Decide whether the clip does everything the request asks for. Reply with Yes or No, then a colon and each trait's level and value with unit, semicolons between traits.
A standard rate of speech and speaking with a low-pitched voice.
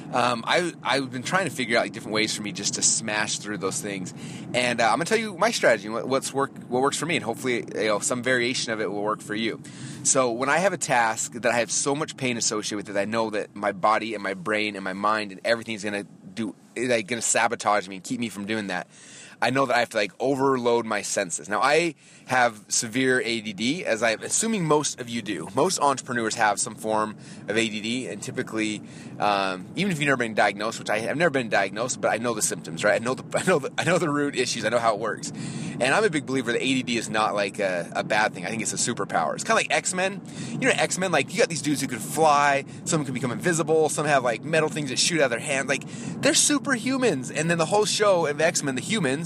No: fast, 265 wpm; low, 130 Hz